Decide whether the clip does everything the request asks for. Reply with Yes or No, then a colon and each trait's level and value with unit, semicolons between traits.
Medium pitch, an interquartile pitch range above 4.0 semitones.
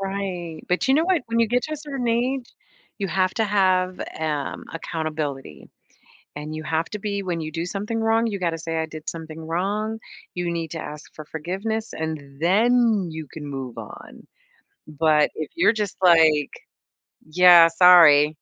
Yes: medium, 175 Hz; average, 5.0 semitones